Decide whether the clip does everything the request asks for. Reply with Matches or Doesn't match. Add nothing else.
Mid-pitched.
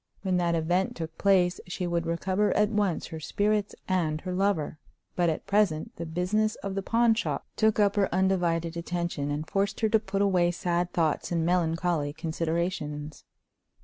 Matches